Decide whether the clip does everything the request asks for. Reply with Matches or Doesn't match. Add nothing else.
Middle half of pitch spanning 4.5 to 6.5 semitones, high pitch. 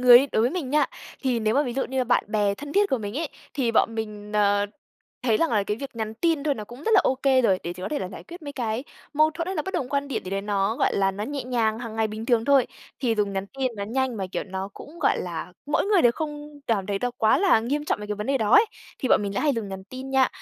Matches